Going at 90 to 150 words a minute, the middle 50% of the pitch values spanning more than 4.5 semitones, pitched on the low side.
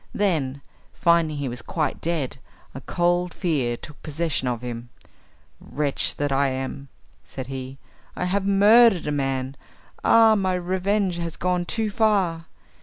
No: average, 145 wpm; wide, 5.5 semitones; medium, 165 Hz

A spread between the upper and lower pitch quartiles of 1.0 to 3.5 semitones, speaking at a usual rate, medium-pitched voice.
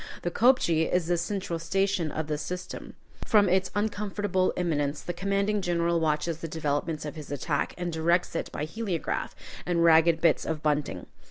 Yes: average, 3.0 semitones; average, 170 wpm; medium, 170 Hz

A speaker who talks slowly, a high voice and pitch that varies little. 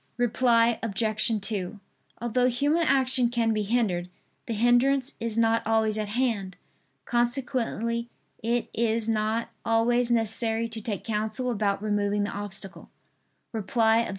Yes: slow, 130 wpm; high, 230 Hz; narrow, 2.0 semitones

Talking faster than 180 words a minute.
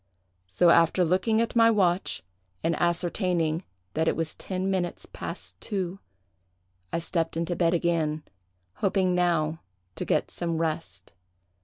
No: slow, 135 wpm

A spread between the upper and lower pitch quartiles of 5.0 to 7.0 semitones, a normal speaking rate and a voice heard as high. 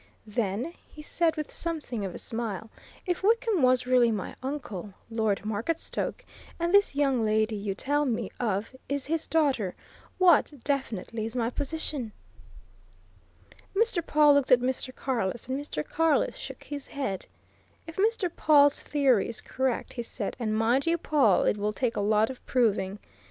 Yes: wide, 5.4 semitones; average, 160 wpm; very high, 255 Hz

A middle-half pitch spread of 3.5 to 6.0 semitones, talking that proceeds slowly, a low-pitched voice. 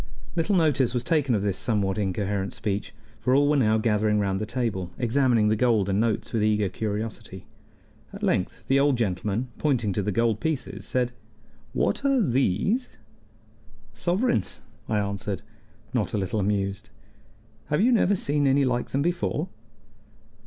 No: wide, 5.4 semitones; average, 160 wpm; low, 115 Hz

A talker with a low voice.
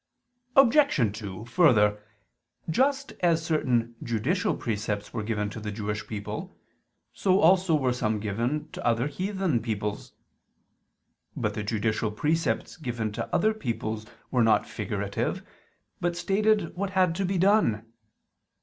Yes: low, 125 Hz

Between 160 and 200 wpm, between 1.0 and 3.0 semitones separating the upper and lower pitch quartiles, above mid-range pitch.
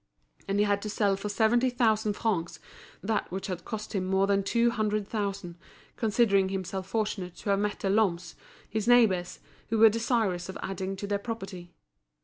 Yes: average, 180 wpm; narrow, 2.4 semitones; high, 200 Hz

